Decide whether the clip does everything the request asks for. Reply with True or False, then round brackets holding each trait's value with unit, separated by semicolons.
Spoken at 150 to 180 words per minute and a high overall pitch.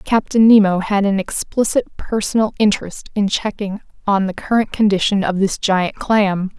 True (155 wpm; 205 Hz)